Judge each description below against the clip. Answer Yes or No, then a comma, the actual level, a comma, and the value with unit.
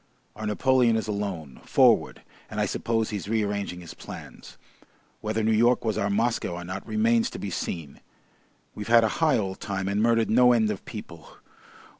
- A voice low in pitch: Yes, low, 110 Hz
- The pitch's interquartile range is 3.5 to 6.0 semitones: No, average, 2.8 semitones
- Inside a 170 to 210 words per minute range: Yes, average, 180 wpm